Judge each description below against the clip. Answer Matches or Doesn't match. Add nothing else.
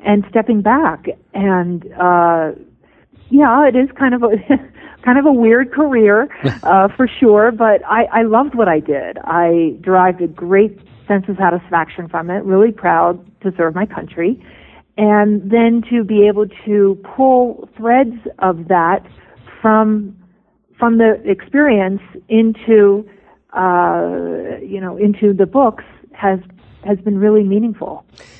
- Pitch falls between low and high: Doesn't match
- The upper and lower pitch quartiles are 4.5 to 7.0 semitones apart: Doesn't match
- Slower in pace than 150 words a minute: Matches